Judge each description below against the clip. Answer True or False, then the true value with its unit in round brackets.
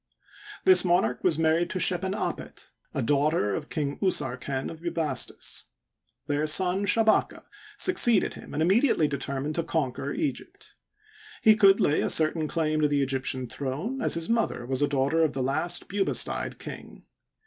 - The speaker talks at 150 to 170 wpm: True (160 wpm)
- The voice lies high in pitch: False (155 Hz)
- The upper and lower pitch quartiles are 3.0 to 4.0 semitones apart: False (4.9 semitones)